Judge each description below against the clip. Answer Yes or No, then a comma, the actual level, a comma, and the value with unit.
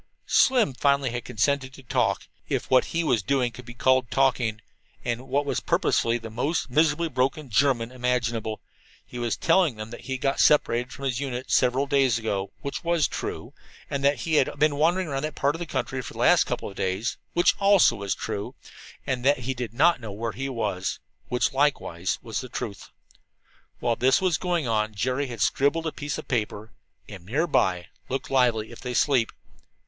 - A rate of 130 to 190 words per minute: No, average, 200 wpm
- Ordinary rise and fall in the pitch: Yes, average, 3.6 semitones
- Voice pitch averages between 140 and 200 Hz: No, low, 130 Hz